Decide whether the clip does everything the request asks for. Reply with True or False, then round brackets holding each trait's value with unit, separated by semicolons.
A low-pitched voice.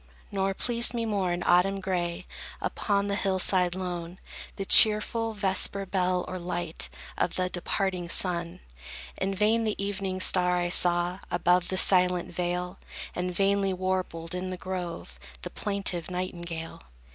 False (185 Hz)